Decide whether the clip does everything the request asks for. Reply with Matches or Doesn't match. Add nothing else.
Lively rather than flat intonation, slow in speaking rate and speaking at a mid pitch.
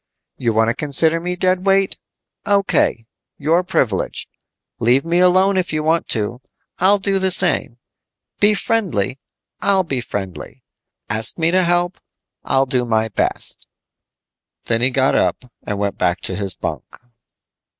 Doesn't match